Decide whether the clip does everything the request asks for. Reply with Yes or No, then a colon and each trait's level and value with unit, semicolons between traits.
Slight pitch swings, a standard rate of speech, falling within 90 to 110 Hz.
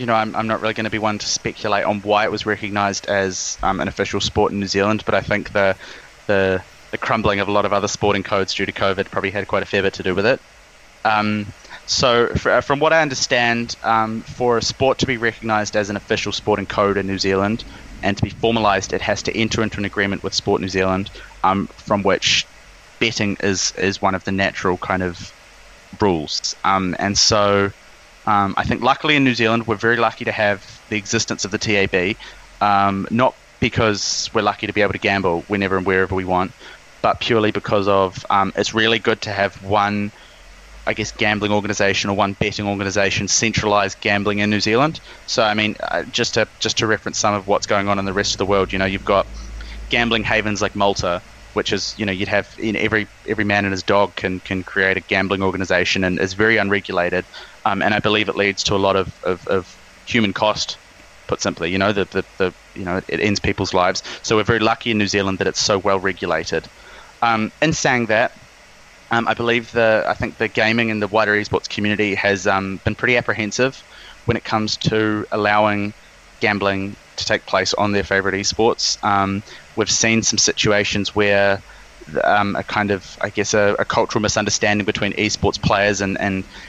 No: narrow, 2.0 semitones; fast, 215 wpm; low, 105 Hz